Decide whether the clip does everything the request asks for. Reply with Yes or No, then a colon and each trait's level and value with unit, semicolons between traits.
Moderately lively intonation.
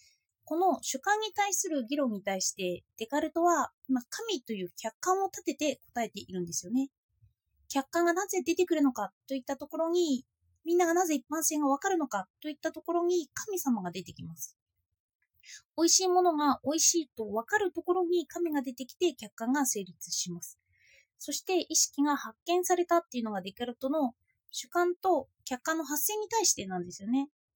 No: wide, 7.8 semitones